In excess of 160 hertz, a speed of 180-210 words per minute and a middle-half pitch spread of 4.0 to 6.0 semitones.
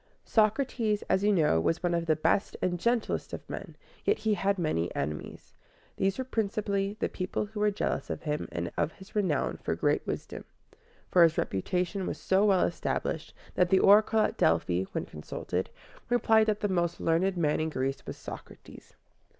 Yes: high, 190 Hz; average, 185 wpm; average, 4.6 semitones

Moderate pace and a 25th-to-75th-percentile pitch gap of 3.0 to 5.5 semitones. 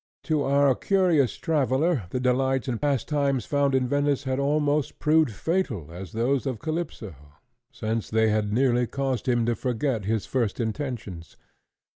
Yes: average, 150 wpm; average, 4.0 semitones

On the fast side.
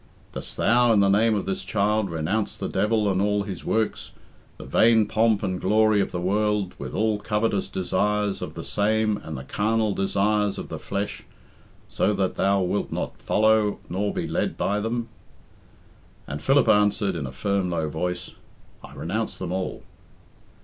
No: average, 175 wpm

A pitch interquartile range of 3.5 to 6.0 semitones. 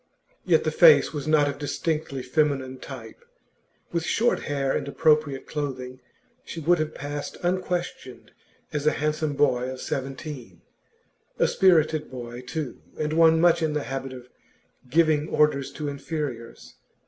No: average, 3.0 semitones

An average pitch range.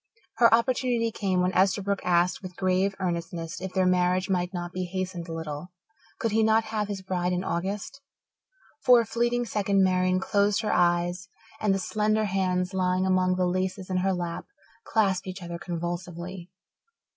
No: narrow, 2.1 semitones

